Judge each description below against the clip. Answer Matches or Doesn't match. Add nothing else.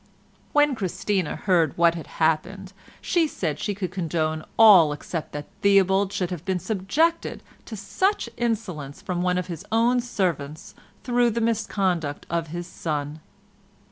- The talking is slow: Doesn't match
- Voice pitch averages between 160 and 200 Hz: Matches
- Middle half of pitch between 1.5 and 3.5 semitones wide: Doesn't match